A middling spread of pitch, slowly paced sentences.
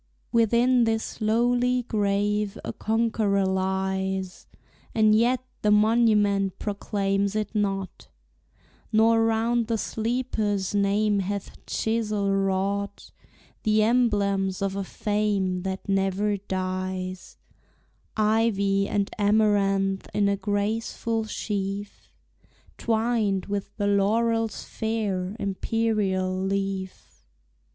No: narrow, 2.2 semitones; slow, 95 wpm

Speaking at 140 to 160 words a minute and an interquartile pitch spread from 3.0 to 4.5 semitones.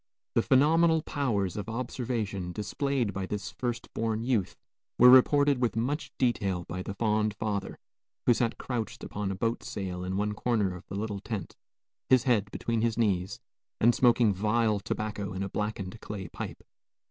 No: average, 170 wpm; average, 3.4 semitones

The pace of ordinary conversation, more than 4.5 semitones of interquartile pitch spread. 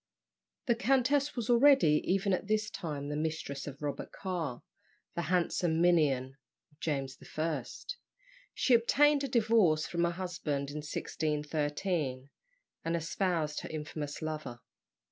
No: slow, 130 wpm; average, 5.0 semitones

